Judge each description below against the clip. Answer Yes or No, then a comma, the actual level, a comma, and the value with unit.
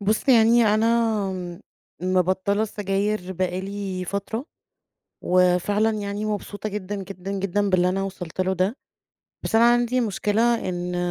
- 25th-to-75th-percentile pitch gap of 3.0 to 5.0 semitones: No, narrow, 2.6 semitones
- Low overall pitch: No, high, 200 Hz